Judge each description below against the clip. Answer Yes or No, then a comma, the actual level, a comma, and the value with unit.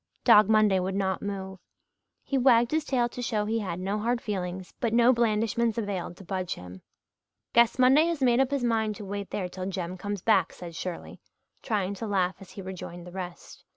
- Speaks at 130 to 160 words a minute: No, fast, 205 wpm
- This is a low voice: No, high, 205 Hz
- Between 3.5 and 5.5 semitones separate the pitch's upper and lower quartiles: Yes, average, 4.0 semitones